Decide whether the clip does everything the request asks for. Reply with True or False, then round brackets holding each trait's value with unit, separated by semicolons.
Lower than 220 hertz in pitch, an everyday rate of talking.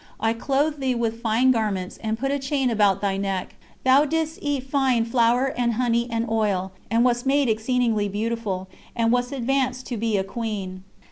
False (235 Hz; 185 wpm)